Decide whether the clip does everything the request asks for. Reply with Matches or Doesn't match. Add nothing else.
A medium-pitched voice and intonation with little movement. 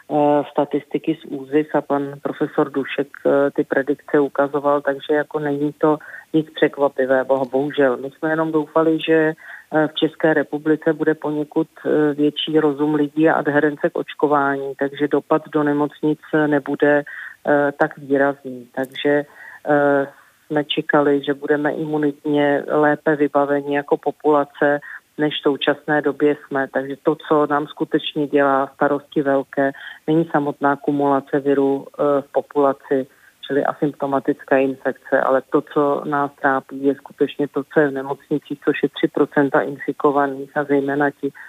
Matches